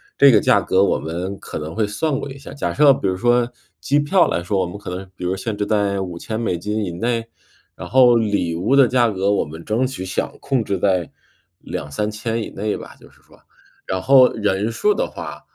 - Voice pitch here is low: Yes, low, 105 Hz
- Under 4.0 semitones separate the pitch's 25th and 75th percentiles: No, average, 4.5 semitones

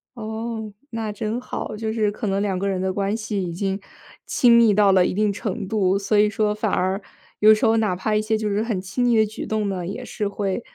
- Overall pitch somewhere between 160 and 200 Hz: No, high, 210 Hz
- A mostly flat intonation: Yes, narrow, 2.0 semitones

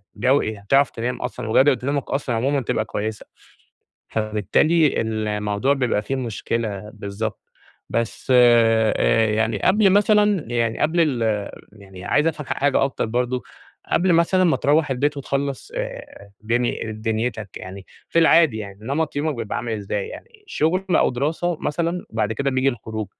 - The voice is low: Yes, low, 125 Hz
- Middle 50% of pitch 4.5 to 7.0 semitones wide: Yes, average, 5.3 semitones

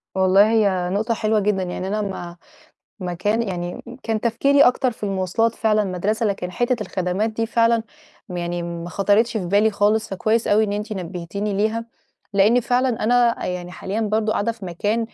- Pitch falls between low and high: No, high, 210 Hz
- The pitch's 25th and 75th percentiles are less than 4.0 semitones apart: Yes, average, 3.3 semitones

